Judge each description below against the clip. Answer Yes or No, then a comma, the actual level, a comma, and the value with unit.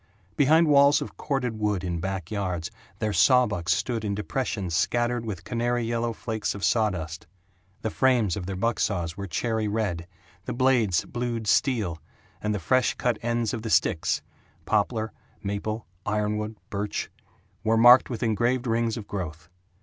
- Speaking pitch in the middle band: No, low, 110 Hz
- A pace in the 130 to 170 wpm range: Yes, average, 160 wpm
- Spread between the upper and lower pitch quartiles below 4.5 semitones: Yes, average, 3.3 semitones